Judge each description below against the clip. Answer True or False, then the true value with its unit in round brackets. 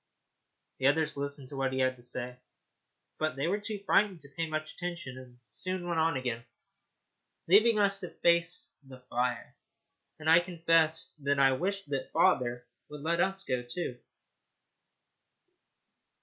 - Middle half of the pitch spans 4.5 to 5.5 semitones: True (5.1 semitones)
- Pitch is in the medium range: True (155 Hz)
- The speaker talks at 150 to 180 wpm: True (155 wpm)